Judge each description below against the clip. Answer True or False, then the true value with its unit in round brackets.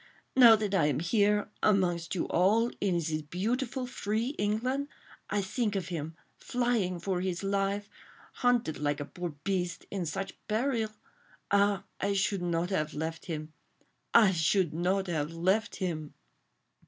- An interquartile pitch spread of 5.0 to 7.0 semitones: False (4.1 semitones)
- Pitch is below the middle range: False (195 Hz)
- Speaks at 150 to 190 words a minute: False (140 wpm)